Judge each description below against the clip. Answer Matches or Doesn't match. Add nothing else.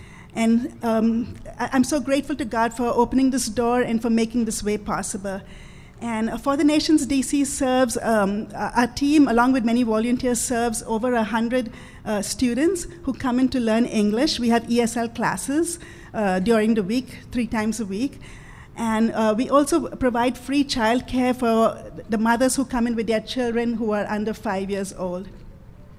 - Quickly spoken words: Doesn't match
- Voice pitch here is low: Doesn't match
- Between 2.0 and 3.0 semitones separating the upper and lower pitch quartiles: Matches